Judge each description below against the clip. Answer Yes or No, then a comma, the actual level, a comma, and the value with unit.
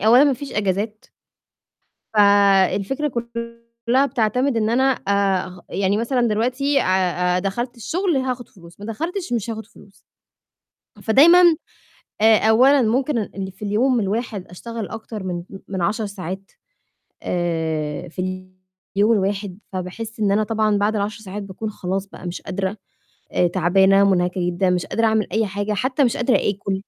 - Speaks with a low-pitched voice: No, high, 210 Hz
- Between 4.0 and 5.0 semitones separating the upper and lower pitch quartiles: No, average, 3.6 semitones